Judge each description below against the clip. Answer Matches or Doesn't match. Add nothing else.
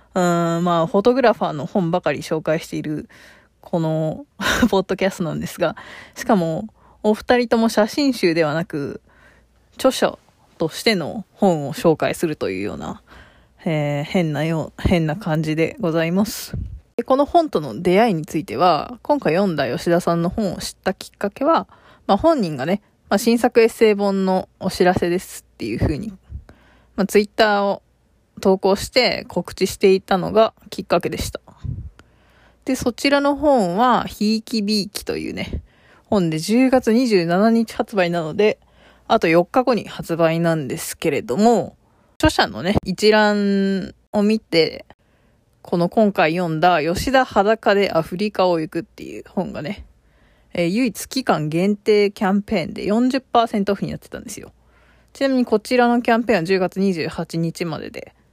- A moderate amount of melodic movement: Matches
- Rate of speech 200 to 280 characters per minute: Doesn't match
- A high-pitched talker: Matches